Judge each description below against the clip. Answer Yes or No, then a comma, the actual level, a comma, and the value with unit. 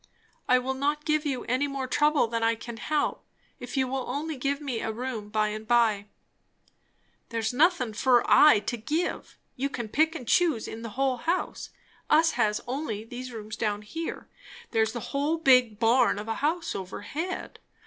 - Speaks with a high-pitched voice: Yes, very high, 250 Hz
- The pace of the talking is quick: No, average, 180 wpm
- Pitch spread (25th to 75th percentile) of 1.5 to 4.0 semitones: No, average, 4.7 semitones